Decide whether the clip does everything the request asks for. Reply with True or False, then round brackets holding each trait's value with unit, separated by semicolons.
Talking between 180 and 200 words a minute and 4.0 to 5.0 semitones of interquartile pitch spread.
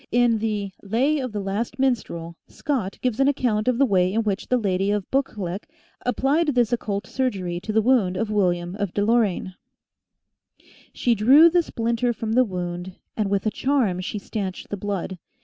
True (185 wpm; 4.4 semitones)